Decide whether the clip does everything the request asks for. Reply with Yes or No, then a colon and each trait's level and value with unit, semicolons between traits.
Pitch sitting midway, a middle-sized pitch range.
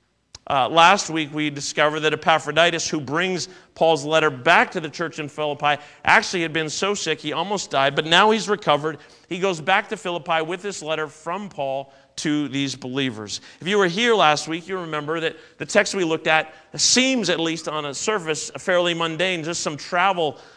Yes: medium, 160 Hz; average, 3.2 semitones